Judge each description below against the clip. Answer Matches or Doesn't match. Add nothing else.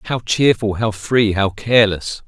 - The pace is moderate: Matches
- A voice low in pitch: Matches